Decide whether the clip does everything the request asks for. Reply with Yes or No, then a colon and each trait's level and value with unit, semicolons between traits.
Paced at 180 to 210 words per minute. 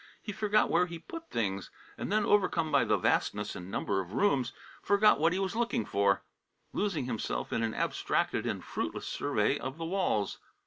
Yes: average, 185 wpm